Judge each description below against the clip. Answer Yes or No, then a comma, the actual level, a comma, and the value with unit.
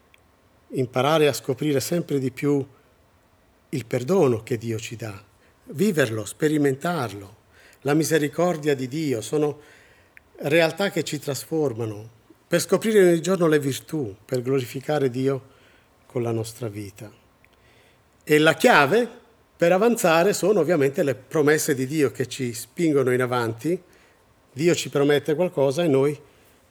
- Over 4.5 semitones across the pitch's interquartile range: Yes, average, 5.1 semitones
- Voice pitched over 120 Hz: Yes, low, 135 Hz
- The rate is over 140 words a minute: No, average, 130 wpm